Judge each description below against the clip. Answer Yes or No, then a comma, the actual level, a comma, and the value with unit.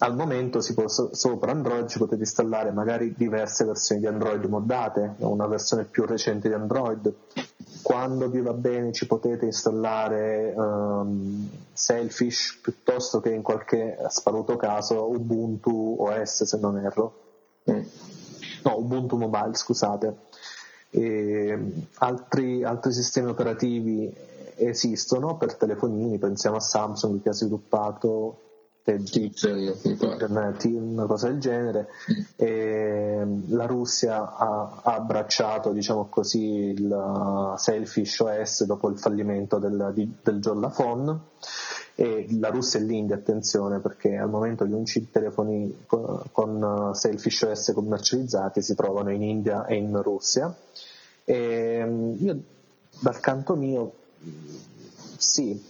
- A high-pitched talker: No, low, 110 Hz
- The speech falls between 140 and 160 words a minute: No, slow, 115 wpm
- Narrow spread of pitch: Yes, narrow, 1.9 semitones